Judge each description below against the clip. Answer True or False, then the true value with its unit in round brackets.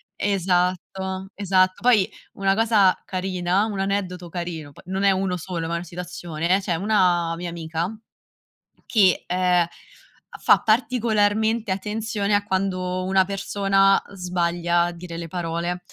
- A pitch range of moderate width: False (2.2 semitones)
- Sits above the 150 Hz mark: True (185 Hz)